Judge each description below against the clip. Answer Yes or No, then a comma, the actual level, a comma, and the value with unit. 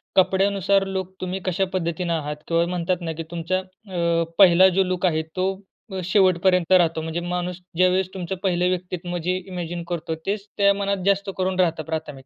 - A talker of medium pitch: Yes, medium, 180 Hz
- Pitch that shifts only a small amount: Yes, narrow, 1.9 semitones